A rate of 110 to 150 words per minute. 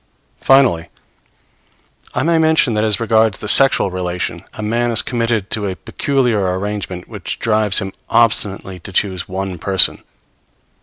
Yes: average, 145 wpm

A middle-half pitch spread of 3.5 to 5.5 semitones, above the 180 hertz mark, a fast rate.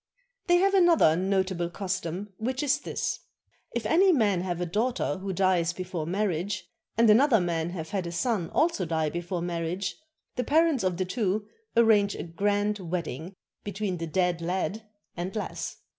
No: average, 4.0 semitones; high, 190 Hz; average, 165 wpm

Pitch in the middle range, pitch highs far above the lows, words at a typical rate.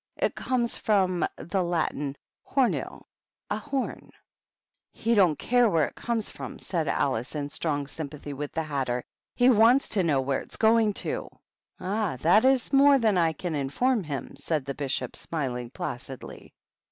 Yes: medium, 170 Hz; wide, 7.9 semitones; average, 165 wpm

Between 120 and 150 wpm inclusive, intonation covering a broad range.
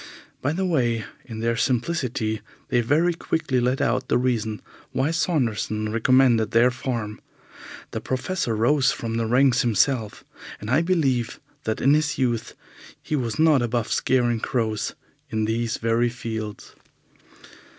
No: average, 140 wpm; average, 3.1 semitones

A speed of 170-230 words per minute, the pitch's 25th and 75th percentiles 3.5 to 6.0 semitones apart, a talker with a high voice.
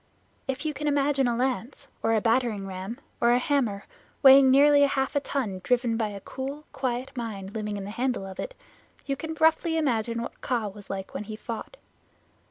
Yes: average, 195 wpm; average, 4.4 semitones; high, 245 Hz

